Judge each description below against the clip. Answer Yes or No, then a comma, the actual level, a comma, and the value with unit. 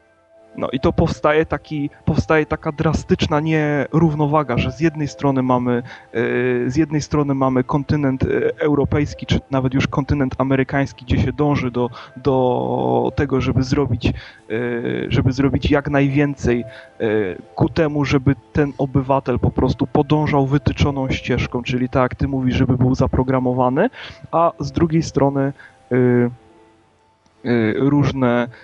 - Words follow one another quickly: No, average, 125 wpm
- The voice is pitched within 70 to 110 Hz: No, low, 135 Hz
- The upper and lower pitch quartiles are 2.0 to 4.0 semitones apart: Yes, average, 3.0 semitones